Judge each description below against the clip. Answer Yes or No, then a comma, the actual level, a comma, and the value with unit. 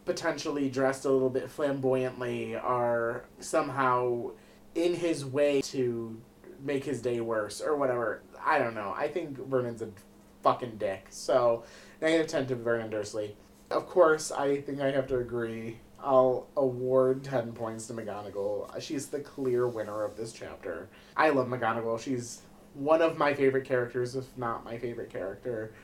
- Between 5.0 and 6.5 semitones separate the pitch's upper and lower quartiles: No, average, 3.2 semitones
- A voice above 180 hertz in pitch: No, low, 125 Hz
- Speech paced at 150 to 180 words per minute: Yes, average, 160 wpm